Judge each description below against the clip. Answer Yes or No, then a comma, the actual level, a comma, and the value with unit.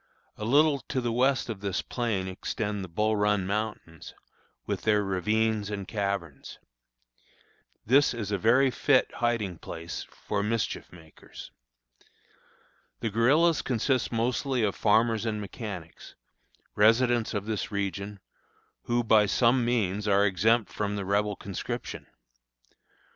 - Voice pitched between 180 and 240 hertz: No, low, 105 Hz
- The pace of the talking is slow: Yes, slow, 130 wpm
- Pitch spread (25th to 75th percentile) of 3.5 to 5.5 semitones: No, average, 3.0 semitones